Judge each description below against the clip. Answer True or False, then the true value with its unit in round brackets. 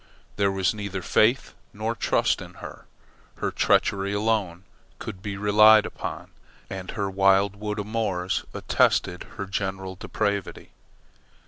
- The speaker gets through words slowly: True (125 wpm)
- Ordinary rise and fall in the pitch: False (1.7 semitones)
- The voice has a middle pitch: False (100 Hz)